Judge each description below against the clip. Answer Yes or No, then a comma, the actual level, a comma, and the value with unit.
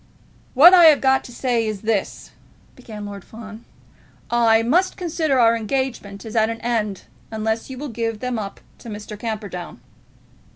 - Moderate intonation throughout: Yes, average, 3.2 semitones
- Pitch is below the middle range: No, high, 225 Hz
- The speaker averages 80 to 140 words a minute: No, average, 165 wpm